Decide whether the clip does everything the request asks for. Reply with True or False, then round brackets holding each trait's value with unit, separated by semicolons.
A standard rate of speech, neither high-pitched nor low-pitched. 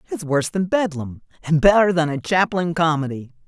True (175 wpm; 160 Hz)